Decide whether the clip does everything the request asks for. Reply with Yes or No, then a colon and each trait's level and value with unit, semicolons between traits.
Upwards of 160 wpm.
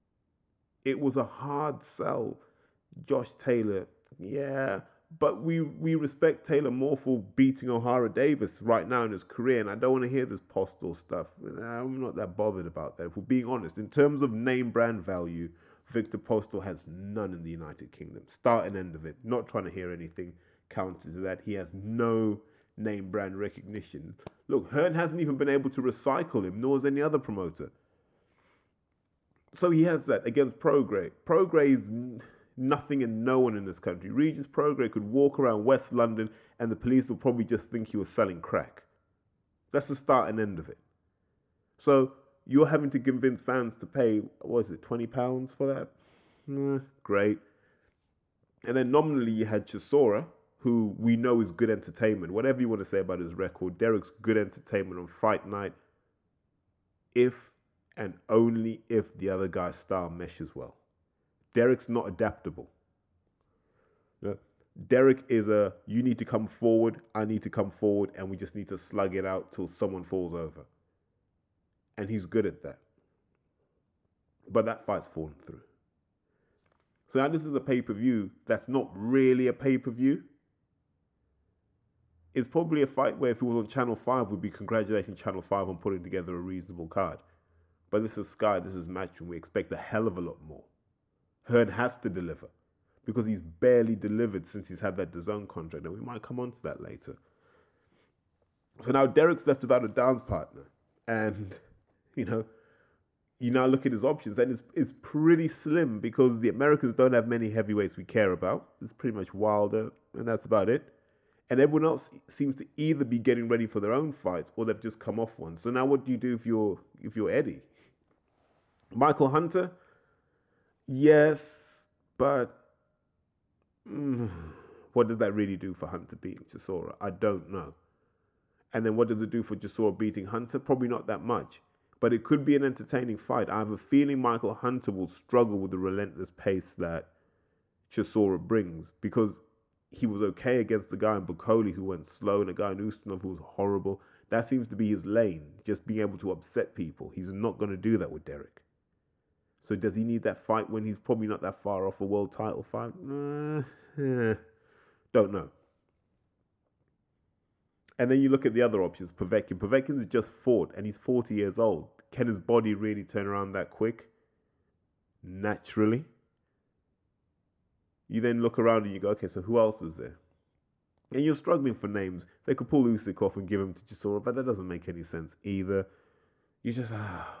Yes: average, 180 wpm